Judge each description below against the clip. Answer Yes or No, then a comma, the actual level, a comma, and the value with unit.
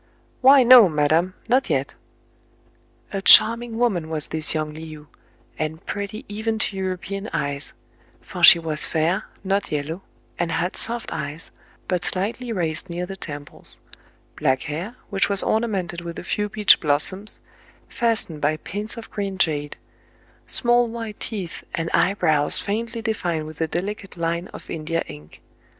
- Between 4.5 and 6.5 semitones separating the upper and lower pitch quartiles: Yes, average, 5.2 semitones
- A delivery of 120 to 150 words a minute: No, average, 160 wpm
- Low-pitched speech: No, medium, 185 Hz